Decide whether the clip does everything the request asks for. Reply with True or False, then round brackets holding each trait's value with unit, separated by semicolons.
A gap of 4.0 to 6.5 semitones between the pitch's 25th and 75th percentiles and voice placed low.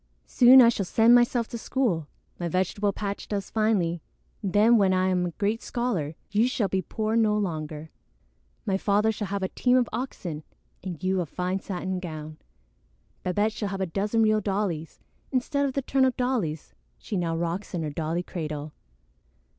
False (4.4 semitones; 195 Hz)